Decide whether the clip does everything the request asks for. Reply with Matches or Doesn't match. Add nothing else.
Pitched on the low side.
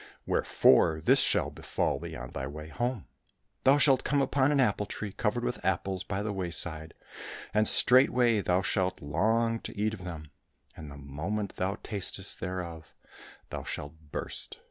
Matches